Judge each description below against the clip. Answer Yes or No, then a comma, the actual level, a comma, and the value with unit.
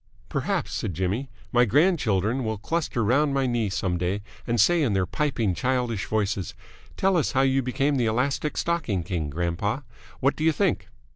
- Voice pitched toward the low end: Yes, low, 120 Hz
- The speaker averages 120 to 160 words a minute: No, average, 175 wpm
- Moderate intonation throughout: No, wide, 5.7 semitones